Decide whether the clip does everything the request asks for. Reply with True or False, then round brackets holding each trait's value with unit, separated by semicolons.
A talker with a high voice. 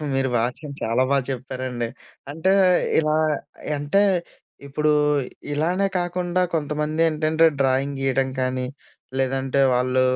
False (140 Hz)